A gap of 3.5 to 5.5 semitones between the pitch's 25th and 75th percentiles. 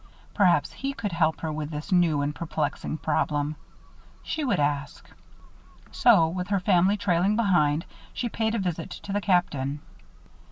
Yes: average, 4.9 semitones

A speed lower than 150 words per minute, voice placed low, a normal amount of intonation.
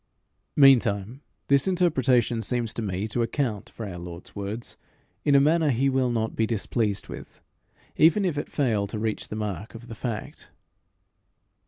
No: average, 165 wpm; low, 115 Hz; average, 4.5 semitones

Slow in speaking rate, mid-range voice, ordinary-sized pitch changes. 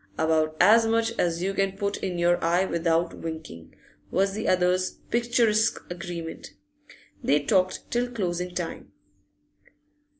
Yes: slow, 130 wpm; medium, 180 Hz; average, 3.3 semitones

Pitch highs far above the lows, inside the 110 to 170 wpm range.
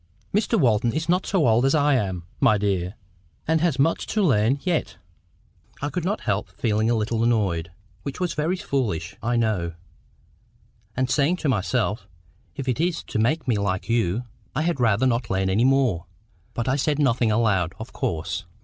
No: wide, 5.9 semitones; average, 180 wpm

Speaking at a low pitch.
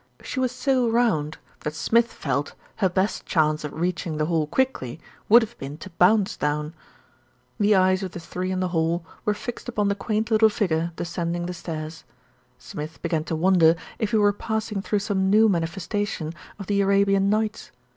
No: medium, 185 Hz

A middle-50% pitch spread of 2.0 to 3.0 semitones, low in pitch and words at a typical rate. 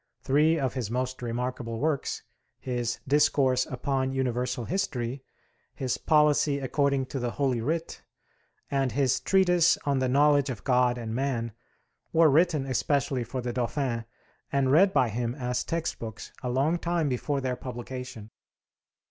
Yes: average, 2.7 semitones; low, 130 Hz; average, 145 wpm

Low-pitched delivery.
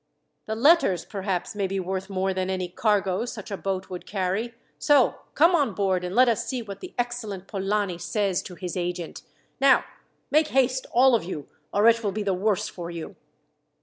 No: high, 200 Hz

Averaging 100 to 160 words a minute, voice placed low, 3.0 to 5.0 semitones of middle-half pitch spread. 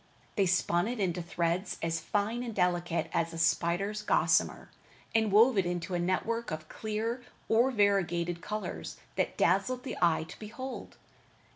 No: average, 155 wpm; high, 195 Hz; average, 4.4 semitones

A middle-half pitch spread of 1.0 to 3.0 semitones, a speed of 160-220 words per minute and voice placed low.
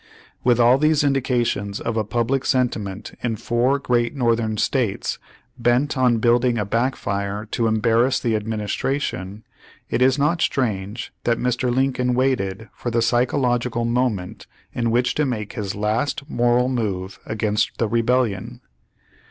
No: average, 2.7 semitones; average, 145 wpm; low, 120 Hz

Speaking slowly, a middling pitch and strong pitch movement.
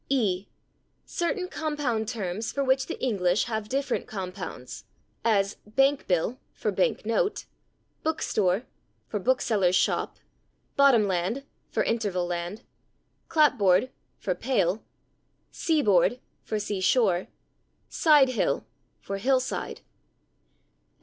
No: slow, 100 wpm; high, 220 Hz; wide, 5.9 semitones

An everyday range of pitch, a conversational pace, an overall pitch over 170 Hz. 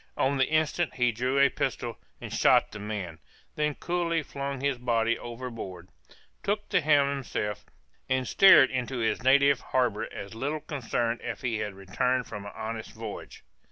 No: average, 4.0 semitones; average, 170 wpm; low, 125 Hz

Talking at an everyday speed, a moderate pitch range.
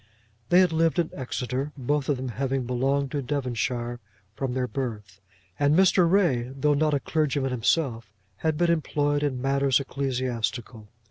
Yes: average, 155 wpm; average, 3.0 semitones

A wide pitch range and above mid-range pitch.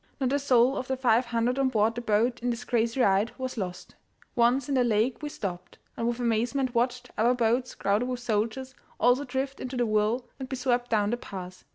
No: narrow, 2.5 semitones; high, 240 Hz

